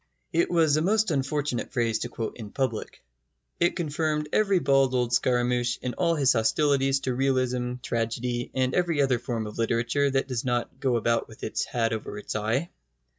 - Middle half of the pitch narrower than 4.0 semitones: Yes, average, 3.4 semitones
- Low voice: Yes, low, 130 Hz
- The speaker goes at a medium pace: Yes, average, 180 wpm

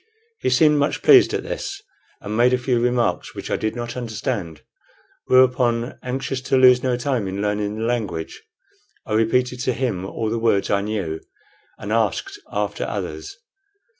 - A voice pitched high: No, low, 120 Hz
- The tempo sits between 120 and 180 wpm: Yes, average, 165 wpm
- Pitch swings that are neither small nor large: Yes, average, 3.2 semitones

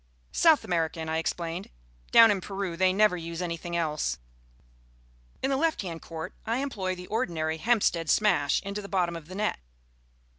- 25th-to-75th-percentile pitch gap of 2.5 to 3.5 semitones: No, average, 4.0 semitones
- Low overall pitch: No, medium, 180 Hz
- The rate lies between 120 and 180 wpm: Yes, average, 170 wpm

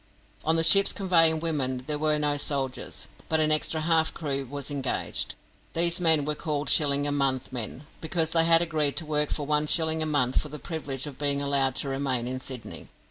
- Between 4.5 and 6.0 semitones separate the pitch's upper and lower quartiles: No, narrow, 2.5 semitones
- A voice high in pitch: No, medium, 150 Hz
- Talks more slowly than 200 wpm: No, fast, 205 wpm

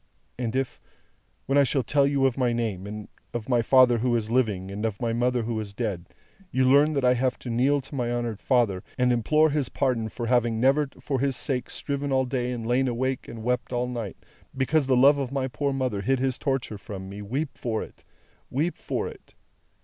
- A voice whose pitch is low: Yes, low, 125 Hz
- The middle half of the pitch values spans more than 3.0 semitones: No, narrow, 2.6 semitones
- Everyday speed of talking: No, fast, 220 wpm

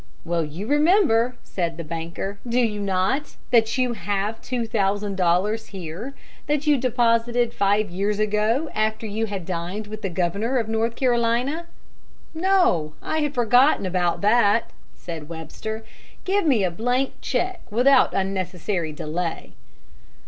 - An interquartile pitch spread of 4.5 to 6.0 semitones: Yes, average, 4.9 semitones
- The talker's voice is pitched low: No, high, 215 Hz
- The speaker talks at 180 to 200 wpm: No, average, 140 wpm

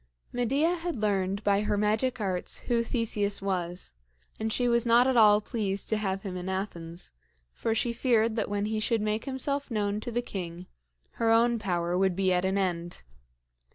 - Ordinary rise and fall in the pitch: Yes, average, 3.5 semitones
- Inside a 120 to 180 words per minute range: No, average, 190 wpm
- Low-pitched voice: No, high, 210 Hz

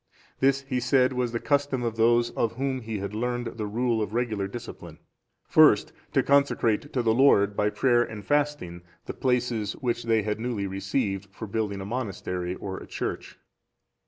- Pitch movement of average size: Yes, average, 3.5 semitones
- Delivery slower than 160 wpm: No, average, 180 wpm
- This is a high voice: No, low, 115 Hz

